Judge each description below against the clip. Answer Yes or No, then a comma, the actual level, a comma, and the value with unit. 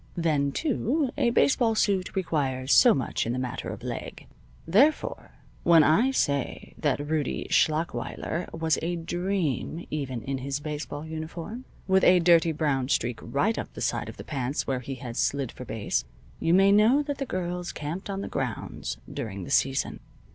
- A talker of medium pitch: Yes, medium, 160 Hz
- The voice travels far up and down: Yes, wide, 5.7 semitones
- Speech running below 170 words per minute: No, average, 175 wpm